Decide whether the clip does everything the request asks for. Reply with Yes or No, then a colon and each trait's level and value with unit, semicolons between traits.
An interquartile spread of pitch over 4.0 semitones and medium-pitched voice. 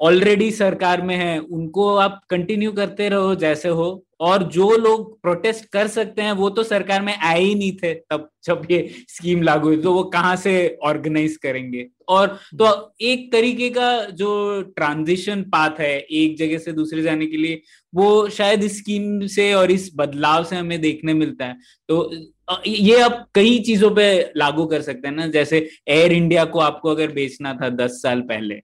Yes: average, 4.6 semitones; medium, 180 Hz